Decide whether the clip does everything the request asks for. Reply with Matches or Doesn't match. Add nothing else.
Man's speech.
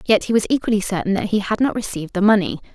Doesn't match